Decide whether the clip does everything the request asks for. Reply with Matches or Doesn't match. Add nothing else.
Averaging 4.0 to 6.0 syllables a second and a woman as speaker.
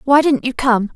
Matches